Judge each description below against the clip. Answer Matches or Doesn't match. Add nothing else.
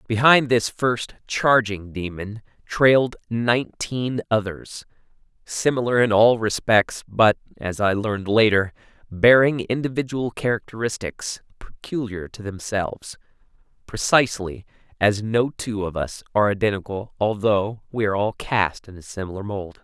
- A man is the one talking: Matches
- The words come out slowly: Matches